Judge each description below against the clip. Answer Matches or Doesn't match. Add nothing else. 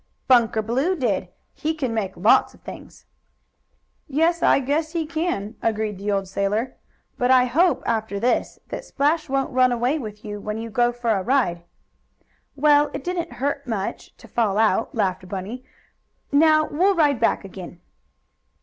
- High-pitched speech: Matches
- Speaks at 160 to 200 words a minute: Matches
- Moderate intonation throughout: Doesn't match